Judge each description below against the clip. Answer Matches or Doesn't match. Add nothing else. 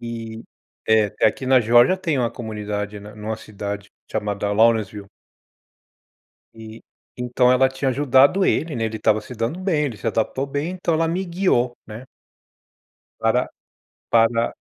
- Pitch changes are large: Doesn't match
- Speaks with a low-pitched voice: Matches